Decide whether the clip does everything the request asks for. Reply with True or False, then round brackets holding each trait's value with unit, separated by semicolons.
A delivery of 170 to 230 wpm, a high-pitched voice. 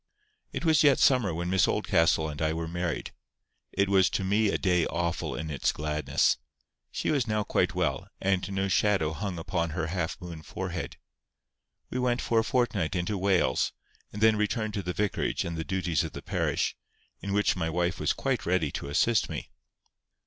False (190 wpm; 90 Hz)